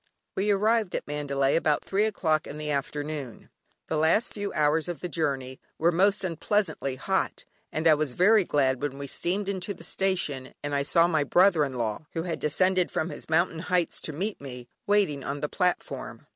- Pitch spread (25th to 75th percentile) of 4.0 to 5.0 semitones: Yes, average, 4.6 semitones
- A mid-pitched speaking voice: Yes, medium, 160 Hz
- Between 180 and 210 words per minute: Yes, average, 195 wpm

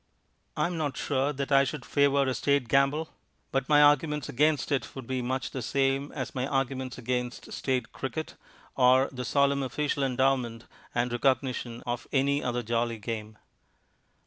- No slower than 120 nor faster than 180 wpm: Yes, average, 165 wpm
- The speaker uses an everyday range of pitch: No, narrow, 2.3 semitones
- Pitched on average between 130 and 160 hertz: Yes, low, 135 Hz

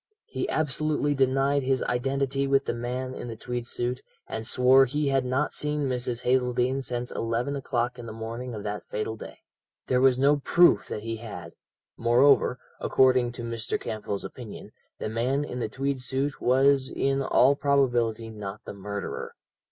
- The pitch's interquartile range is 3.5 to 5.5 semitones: No, average, 2.7 semitones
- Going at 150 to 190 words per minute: Yes, average, 170 wpm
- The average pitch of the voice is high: No, low, 125 Hz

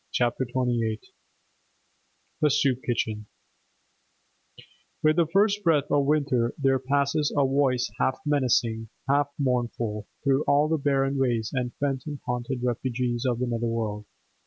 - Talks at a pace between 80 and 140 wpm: Yes, slow, 135 wpm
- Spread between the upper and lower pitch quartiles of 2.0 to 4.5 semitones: Yes, average, 3.1 semitones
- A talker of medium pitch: No, low, 130 Hz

